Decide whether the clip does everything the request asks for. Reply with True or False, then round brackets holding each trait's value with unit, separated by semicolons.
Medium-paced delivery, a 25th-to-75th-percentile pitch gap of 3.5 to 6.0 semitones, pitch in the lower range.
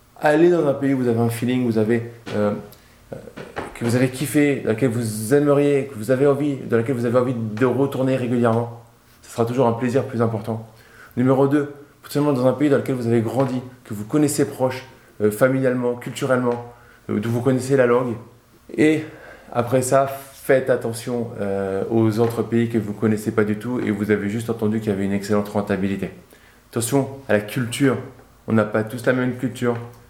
False (205 wpm; 2.9 semitones; 120 Hz)